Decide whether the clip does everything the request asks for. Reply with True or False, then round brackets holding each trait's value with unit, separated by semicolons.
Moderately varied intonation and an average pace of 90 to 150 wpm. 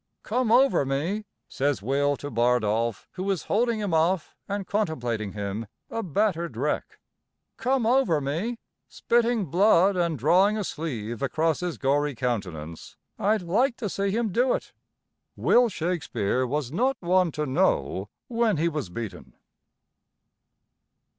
False (8.0 semitones; 140 wpm)